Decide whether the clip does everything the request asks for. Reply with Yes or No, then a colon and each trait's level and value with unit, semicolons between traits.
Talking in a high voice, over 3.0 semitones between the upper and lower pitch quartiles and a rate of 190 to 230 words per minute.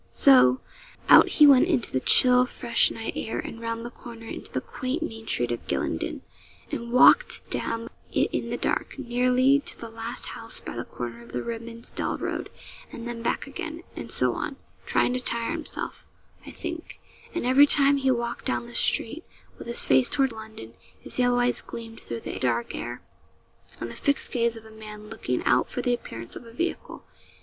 No: high, 235 Hz; narrow, 2.6 semitones; average, 195 wpm